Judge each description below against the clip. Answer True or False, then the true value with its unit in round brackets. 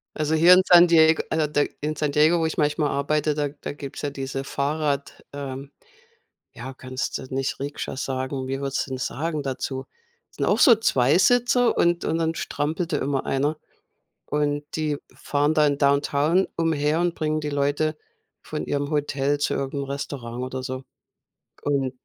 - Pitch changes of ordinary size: False (2.3 semitones)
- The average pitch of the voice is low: False (145 Hz)